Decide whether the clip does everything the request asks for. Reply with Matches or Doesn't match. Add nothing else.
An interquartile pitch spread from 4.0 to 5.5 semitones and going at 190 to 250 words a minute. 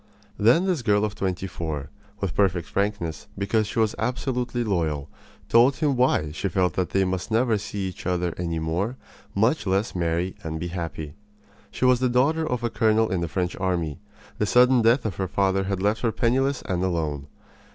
Matches